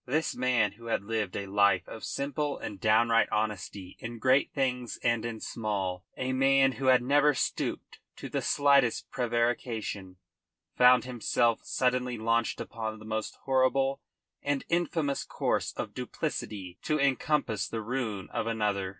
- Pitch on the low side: Yes, low, 120 Hz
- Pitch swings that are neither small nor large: Yes, average, 3.5 semitones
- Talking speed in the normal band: Yes, average, 150 wpm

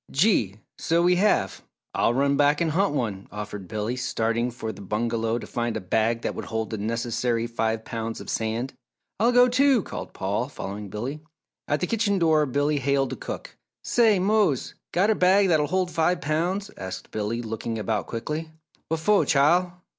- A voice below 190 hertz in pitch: Yes, low, 135 Hz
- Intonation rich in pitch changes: Yes, wide, 7.8 semitones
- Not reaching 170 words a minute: No, average, 180 wpm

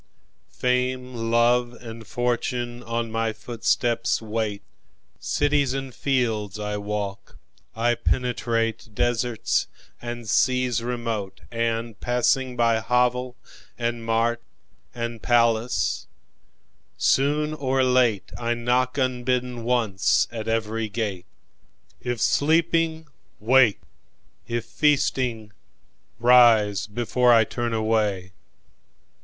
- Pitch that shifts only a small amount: Yes, narrow, 1.9 semitones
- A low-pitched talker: Yes, low, 120 Hz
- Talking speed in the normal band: No, slow, 80 wpm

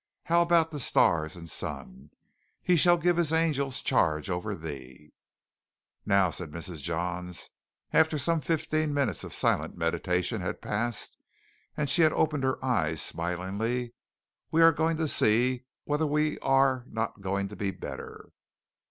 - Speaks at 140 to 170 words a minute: Yes, average, 145 wpm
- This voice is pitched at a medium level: No, low, 125 Hz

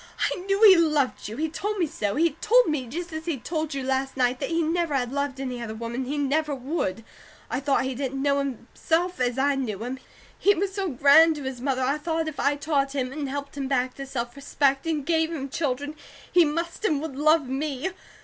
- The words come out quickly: Yes, fast, 235 wpm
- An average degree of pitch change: Yes, average, 3.4 semitones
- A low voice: No, very high, 280 Hz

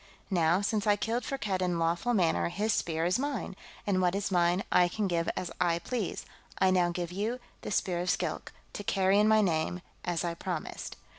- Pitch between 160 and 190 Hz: Yes, medium, 185 Hz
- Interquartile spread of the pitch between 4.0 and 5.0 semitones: No, average, 3.1 semitones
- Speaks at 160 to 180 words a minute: No, fast, 205 wpm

